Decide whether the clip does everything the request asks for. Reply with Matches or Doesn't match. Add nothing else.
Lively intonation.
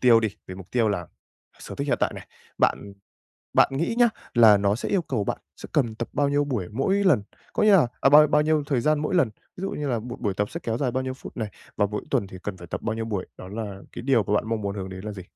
Matches